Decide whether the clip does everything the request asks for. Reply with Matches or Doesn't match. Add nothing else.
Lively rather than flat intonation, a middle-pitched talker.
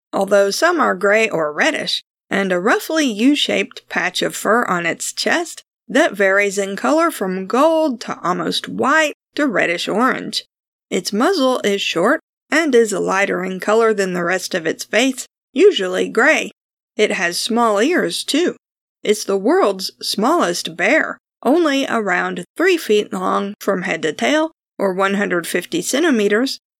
Doesn't match